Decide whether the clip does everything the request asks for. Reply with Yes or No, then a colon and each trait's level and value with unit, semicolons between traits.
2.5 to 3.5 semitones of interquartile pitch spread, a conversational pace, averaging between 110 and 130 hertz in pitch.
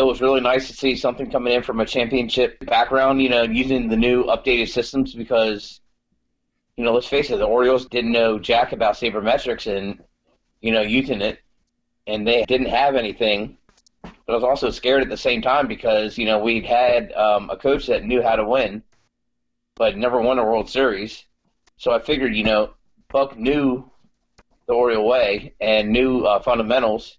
Yes: average, 2.9 semitones; average, 190 wpm; low, 120 Hz